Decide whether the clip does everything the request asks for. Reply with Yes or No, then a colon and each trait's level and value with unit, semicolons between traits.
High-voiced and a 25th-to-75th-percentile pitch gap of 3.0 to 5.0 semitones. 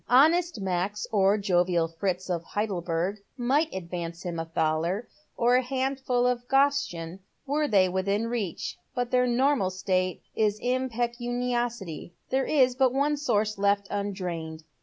No: high, 210 Hz; wide, 5.5 semitones